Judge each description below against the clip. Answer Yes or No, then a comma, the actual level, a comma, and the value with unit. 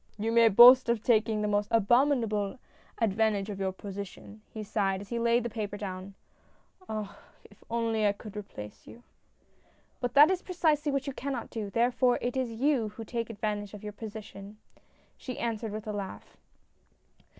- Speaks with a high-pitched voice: Yes, high, 220 Hz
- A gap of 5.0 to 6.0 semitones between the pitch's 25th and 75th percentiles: No, average, 2.7 semitones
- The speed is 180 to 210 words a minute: Yes, average, 185 wpm